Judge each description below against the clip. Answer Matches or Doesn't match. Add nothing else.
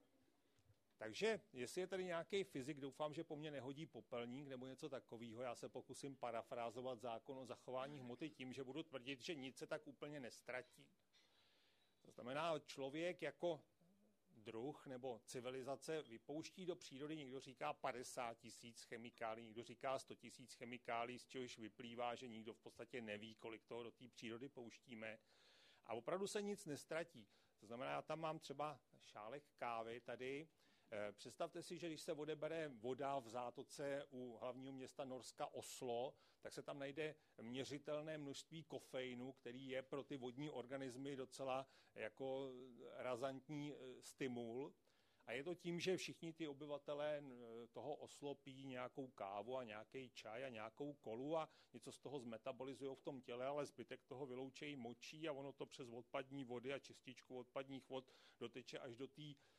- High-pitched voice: Doesn't match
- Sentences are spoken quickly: Doesn't match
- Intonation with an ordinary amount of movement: Matches